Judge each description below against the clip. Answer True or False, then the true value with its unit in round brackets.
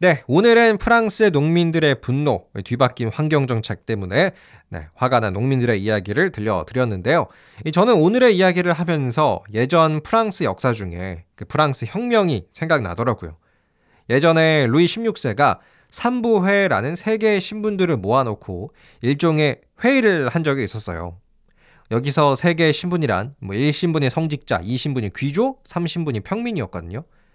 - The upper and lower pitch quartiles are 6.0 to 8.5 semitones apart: True (7.7 semitones)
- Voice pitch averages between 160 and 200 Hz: False (145 Hz)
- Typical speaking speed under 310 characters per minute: False (320 characters per minute)